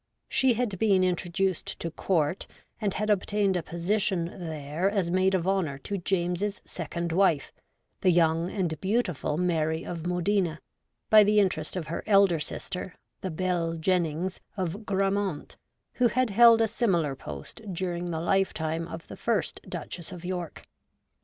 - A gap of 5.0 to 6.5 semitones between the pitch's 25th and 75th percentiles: No, average, 2.9 semitones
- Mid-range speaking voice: Yes, medium, 180 Hz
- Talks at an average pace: Yes, average, 155 wpm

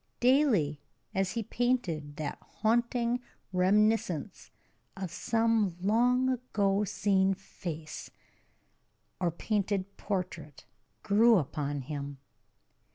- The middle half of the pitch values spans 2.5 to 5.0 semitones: No, wide, 5.5 semitones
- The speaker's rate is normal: No, slow, 90 wpm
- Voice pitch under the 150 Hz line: No, high, 195 Hz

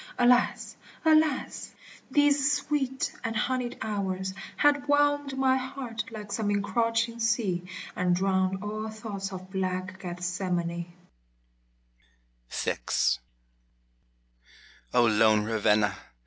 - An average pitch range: No, wide, 5.9 semitones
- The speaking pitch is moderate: No, high, 210 Hz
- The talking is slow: Yes, slow, 95 wpm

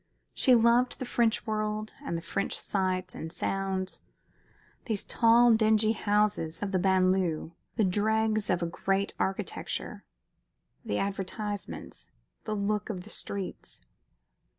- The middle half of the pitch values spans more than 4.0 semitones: No, narrow, 2.6 semitones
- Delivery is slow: Yes, slow, 130 wpm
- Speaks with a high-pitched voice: Yes, high, 205 Hz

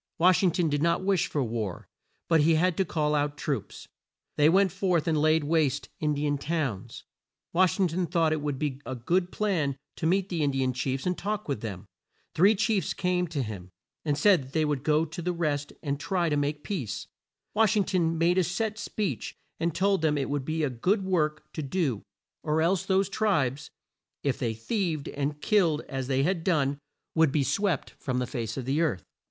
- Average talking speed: No, fast, 215 wpm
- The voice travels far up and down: No, average, 4.4 semitones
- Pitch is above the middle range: No, medium, 155 Hz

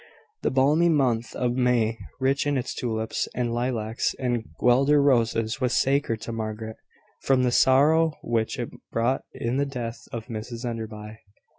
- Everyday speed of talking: Yes, average, 155 wpm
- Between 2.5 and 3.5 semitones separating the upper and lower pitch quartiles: Yes, average, 2.9 semitones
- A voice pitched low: Yes, low, 120 Hz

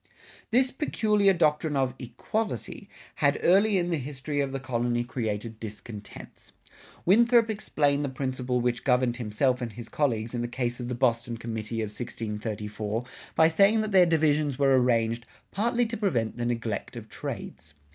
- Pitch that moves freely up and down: Yes, wide, 5.9 semitones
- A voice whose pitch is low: Yes, low, 130 Hz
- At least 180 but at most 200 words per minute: No, average, 165 wpm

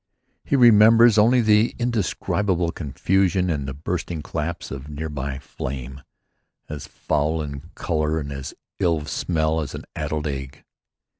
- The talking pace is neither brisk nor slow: Yes, average, 145 wpm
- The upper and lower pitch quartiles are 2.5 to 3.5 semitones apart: No, average, 5.1 semitones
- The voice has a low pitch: Yes, very low, 80 Hz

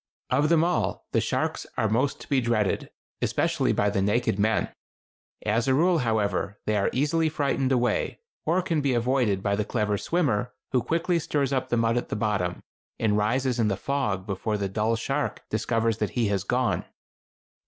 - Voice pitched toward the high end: No, low, 115 Hz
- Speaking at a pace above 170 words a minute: Yes, average, 185 wpm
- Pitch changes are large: No, average, 4.7 semitones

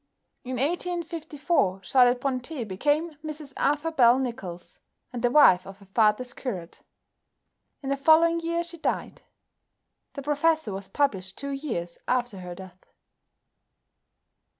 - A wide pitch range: Yes, wide, 7.5 semitones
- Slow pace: Yes, slow, 125 wpm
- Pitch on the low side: No, very high, 265 Hz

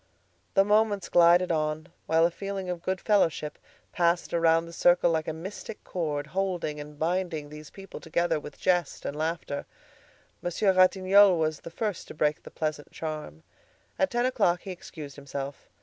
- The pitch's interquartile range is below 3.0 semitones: No, average, 3.4 semitones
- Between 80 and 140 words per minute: No, average, 165 wpm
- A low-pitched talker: No, medium, 170 Hz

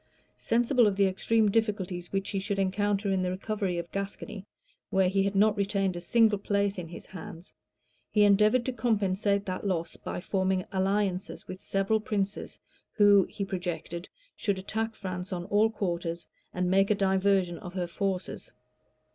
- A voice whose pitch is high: Yes, high, 195 Hz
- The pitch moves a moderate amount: No, narrow, 1.9 semitones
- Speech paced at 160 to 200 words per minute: Yes, average, 165 wpm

